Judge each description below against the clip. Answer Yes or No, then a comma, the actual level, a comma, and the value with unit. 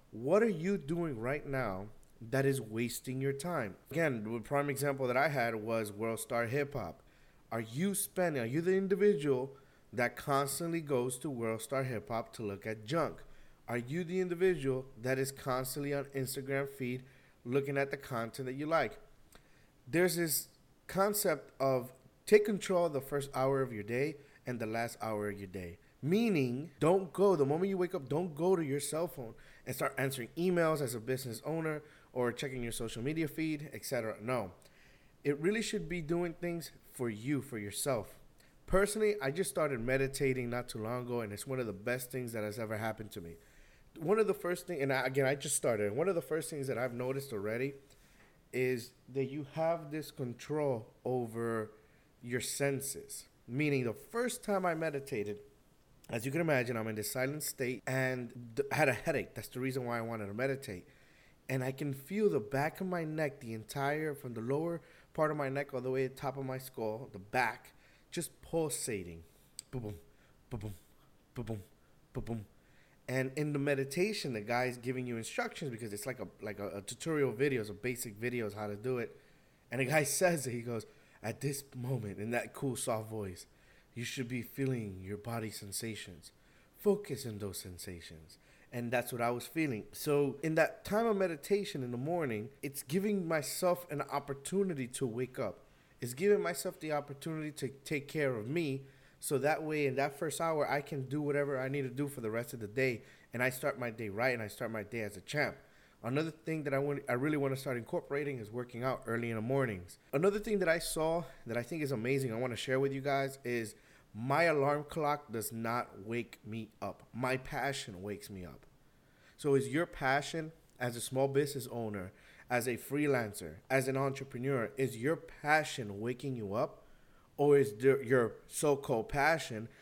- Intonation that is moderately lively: Yes, average, 4.1 semitones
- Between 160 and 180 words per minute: No, average, 200 wpm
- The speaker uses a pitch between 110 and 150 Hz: Yes, low, 135 Hz